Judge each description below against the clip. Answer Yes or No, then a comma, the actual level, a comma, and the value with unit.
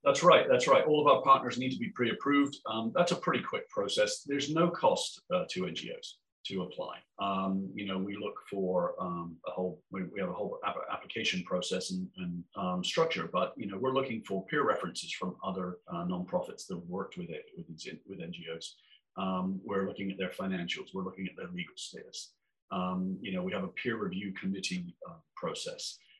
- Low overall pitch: Yes, low, 105 Hz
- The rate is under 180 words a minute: No, average, 200 wpm